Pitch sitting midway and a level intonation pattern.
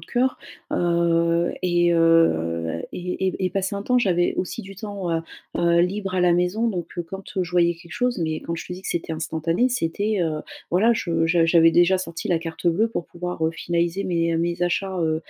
Yes: medium, 175 Hz; narrow, 2.2 semitones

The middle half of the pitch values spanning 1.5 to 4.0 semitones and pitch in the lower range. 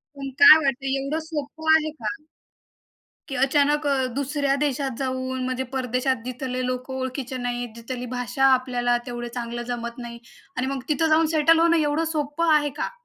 No: average, 2.8 semitones; very high, 265 Hz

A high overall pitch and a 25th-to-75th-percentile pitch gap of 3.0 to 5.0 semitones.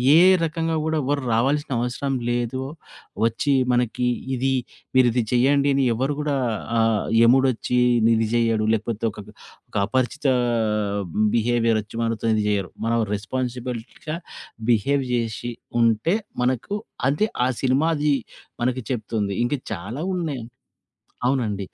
No: low, 125 Hz; average, 3.4 semitones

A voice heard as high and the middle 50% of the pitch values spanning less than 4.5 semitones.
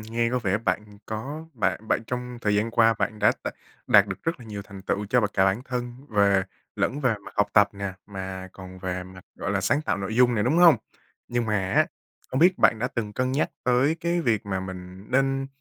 No: low, 110 Hz; average, 4.1 semitones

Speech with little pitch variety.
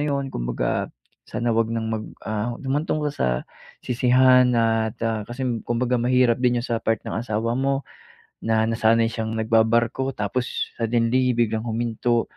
Yes: narrow, 2.1 semitones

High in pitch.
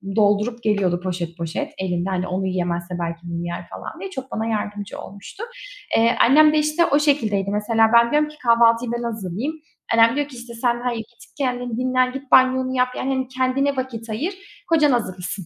Yes: high, 235 Hz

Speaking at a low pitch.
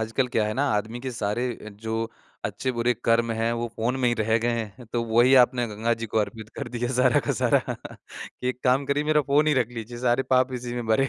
Yes: low, 120 Hz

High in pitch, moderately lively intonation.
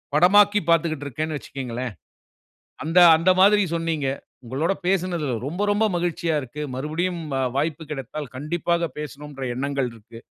No: medium, 155 Hz; average, 3.8 semitones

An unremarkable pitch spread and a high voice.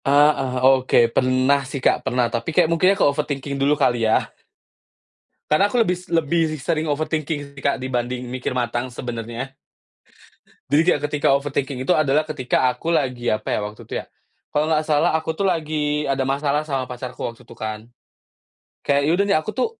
No: average, 3.4 semitones; medium, 140 Hz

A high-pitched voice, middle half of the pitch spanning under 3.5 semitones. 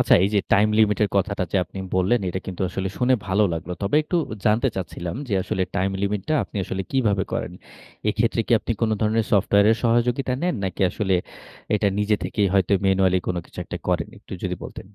No: low, 100 Hz; average, 2.8 semitones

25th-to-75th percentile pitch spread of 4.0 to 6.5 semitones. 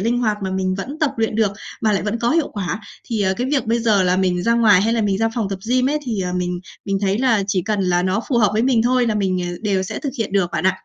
No: average, 3.6 semitones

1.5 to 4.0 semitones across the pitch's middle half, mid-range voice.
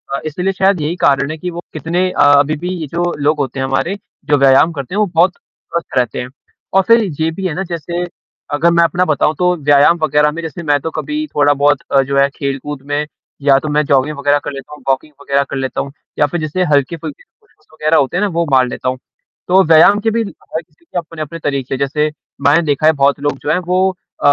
Yes: average, 3.5 semitones; medium, 150 Hz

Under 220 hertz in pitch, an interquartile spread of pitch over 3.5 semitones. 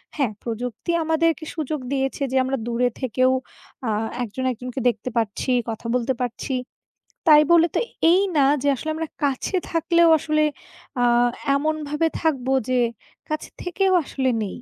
No: very high, 270 Hz; average, 4.1 semitones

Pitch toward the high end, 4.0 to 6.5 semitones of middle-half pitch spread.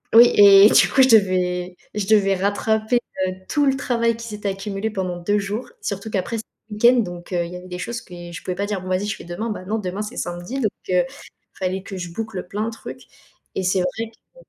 No: high, 200 Hz; average, 3.3 semitones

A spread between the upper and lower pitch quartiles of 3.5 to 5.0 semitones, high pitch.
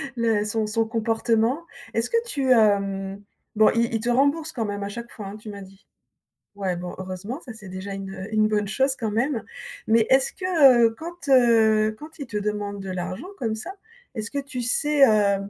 Yes: average, 4.0 semitones; high, 220 Hz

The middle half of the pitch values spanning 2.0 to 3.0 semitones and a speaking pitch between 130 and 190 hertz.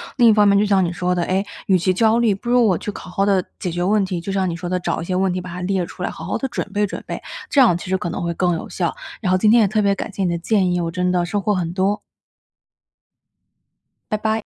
Yes: narrow, 2.6 semitones; medium, 185 Hz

